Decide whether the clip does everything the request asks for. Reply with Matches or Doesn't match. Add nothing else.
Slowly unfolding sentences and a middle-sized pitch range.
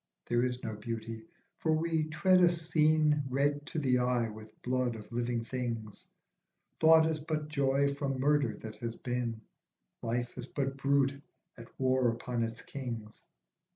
Doesn't match